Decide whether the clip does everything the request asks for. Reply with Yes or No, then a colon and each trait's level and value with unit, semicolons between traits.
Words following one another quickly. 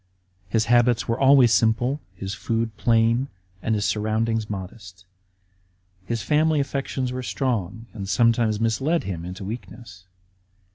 No: slow, 135 wpm